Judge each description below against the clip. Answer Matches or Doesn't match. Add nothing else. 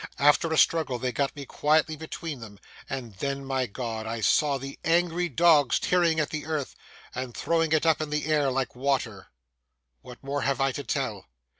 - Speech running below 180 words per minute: Doesn't match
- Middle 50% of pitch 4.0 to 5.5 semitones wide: Doesn't match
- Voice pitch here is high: Doesn't match